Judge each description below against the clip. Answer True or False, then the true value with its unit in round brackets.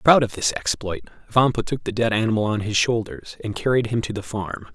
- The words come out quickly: True (230 wpm)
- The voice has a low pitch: True (110 Hz)